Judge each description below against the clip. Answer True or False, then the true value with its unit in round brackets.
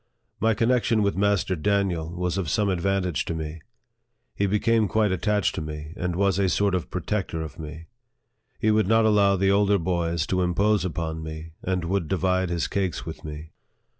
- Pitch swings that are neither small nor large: True (3.5 semitones)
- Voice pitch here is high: False (95 Hz)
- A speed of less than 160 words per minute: False (190 wpm)